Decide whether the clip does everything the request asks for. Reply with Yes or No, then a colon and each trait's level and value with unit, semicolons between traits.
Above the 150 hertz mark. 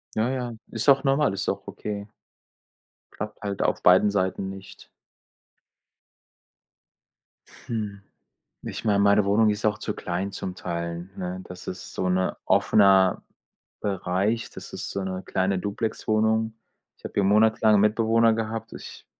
No: low, 100 Hz